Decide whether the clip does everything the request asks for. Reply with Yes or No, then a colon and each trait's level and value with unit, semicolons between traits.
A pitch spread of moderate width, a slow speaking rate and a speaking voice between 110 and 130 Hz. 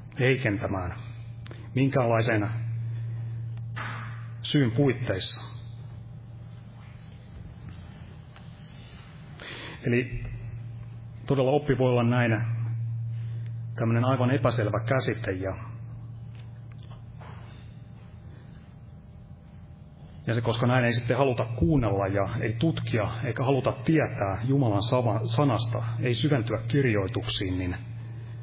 No: narrow, 1.3 semitones; slow, 75 wpm; low, 115 Hz